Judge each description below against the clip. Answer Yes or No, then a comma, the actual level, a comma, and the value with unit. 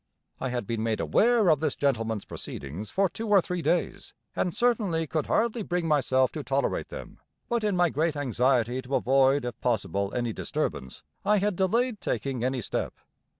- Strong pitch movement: Yes, wide, 7.4 semitones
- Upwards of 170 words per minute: Yes, average, 180 wpm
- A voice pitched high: No, medium, 145 Hz